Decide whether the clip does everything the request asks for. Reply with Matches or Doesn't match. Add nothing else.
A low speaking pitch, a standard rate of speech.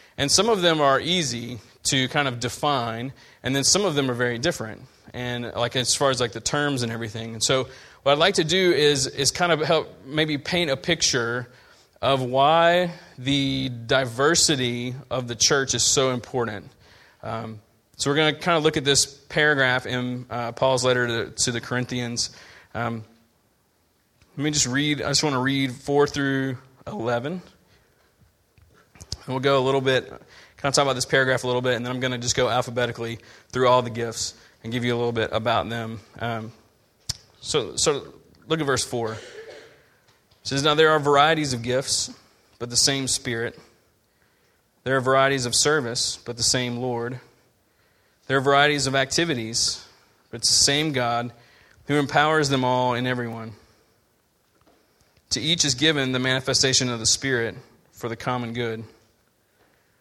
Matches